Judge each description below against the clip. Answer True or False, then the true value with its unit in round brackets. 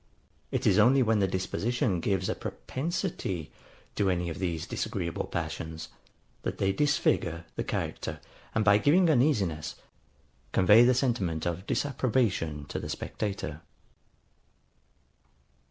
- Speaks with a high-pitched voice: False (100 Hz)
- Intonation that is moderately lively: False (6.1 semitones)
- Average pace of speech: False (120 wpm)